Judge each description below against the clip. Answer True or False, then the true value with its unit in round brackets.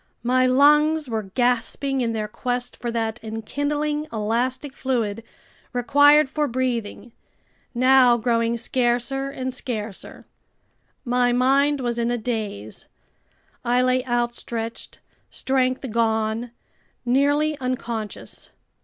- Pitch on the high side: True (245 Hz)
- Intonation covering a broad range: False (2.5 semitones)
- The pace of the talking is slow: True (105 wpm)